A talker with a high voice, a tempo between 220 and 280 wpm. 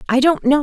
No: very high, 280 Hz; fast, 290 wpm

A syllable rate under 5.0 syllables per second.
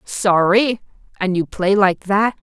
Yes: 3.6 syllables/s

